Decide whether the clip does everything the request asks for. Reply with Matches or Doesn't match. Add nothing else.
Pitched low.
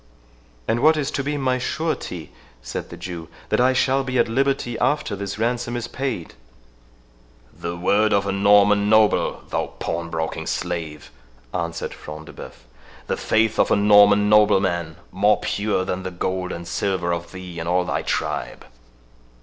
Matches